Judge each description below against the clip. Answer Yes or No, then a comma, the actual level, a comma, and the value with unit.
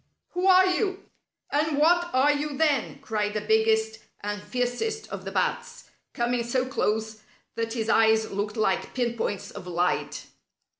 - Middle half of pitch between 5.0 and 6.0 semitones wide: Yes, average, 5.3 semitones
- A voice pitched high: Yes, high, 235 Hz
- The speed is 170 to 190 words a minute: No, average, 155 wpm